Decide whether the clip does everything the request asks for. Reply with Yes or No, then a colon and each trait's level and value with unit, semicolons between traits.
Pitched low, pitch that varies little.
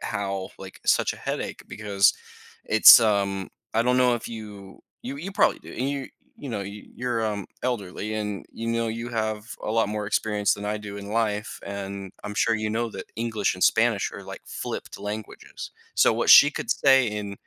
Yes: low, 105 Hz; narrow, 2.3 semitones